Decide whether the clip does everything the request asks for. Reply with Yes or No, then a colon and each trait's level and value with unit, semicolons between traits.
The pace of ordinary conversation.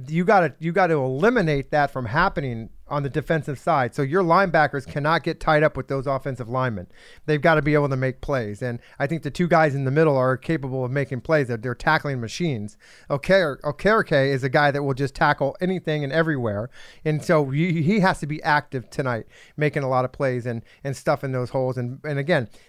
No: fast, 220 wpm